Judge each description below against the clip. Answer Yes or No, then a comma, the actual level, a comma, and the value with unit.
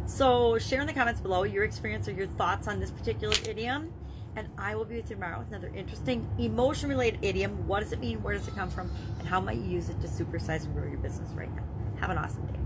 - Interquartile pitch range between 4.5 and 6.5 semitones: No, average, 3.5 semitones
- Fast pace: Yes, fast, 260 wpm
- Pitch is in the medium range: No, low, 110 Hz